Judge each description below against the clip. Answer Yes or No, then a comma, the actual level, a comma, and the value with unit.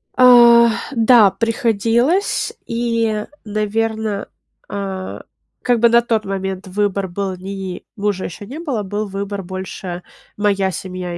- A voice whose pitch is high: Yes, high, 205 Hz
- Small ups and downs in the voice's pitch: No, average, 3.2 semitones